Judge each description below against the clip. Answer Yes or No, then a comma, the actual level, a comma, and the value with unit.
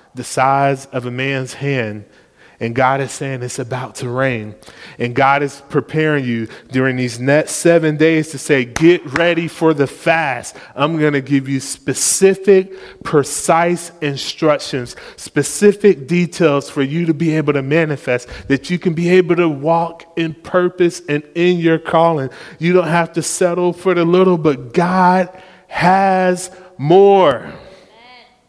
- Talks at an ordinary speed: Yes, average, 155 wpm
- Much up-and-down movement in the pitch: No, average, 4.4 semitones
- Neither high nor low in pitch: Yes, medium, 155 Hz